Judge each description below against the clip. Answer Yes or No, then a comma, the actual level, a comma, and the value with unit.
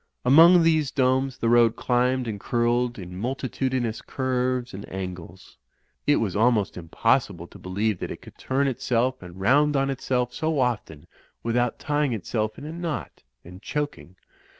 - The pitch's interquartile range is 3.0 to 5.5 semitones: Yes, average, 4.0 semitones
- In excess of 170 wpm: No, average, 160 wpm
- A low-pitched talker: Yes, low, 125 Hz